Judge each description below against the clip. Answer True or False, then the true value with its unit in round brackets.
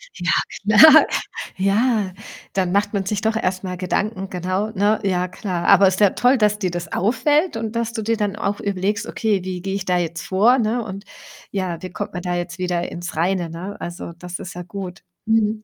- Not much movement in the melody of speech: False (3.1 semitones)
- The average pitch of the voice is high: True (195 Hz)